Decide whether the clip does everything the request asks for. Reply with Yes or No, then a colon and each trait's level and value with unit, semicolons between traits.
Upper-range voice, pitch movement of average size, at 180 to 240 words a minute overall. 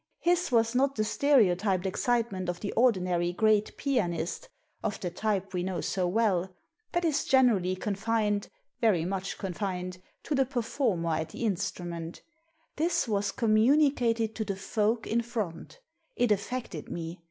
No: high, 210 Hz; average, 4.6 semitones; average, 160 wpm